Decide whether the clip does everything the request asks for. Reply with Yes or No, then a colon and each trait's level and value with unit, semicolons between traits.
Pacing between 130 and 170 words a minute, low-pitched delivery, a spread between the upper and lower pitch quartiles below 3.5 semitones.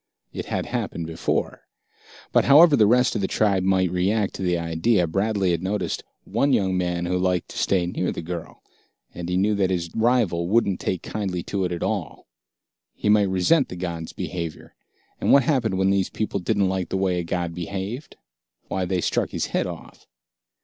No: average, 195 wpm; very low, 95 Hz; average, 2.9 semitones